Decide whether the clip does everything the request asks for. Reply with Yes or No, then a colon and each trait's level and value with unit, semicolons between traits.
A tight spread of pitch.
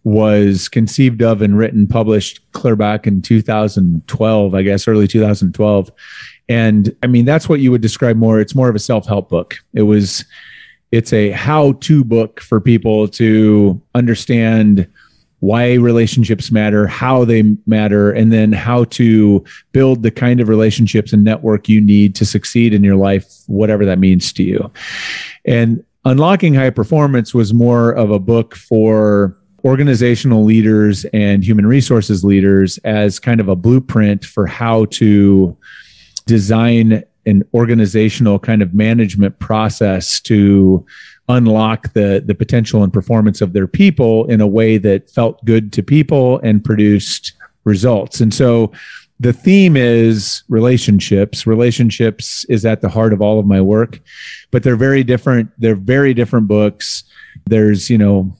Yes: narrow, 2.3 semitones